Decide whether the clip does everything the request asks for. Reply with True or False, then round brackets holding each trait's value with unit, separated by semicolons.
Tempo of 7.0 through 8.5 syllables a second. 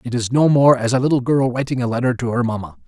False (6.6 syllables/s)